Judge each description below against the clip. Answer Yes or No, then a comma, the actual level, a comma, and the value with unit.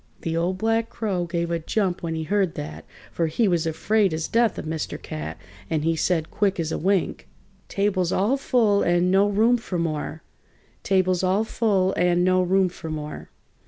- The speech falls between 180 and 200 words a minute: Yes, average, 190 wpm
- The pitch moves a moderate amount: Yes, average, 3.7 semitones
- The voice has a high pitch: No, medium, 180 Hz